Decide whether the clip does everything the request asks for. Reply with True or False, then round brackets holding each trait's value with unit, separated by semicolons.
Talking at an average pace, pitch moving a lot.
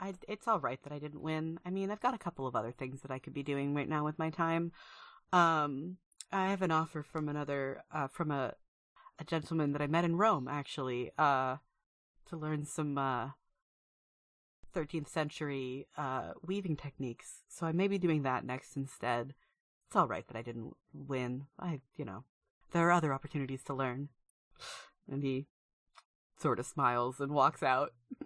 False (185 wpm; 3.8 semitones)